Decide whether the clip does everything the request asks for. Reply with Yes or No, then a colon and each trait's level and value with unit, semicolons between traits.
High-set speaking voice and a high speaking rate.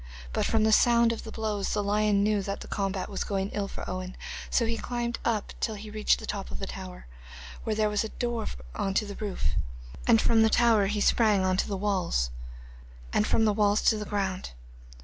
Yes: high, 210 Hz; fast, 225 wpm